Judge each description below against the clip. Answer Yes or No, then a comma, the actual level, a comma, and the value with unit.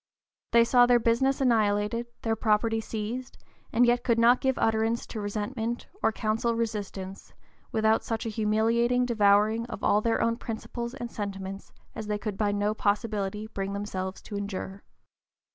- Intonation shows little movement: Yes, narrow, 2.2 semitones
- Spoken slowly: No, average, 160 wpm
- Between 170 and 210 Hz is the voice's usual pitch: No, high, 220 Hz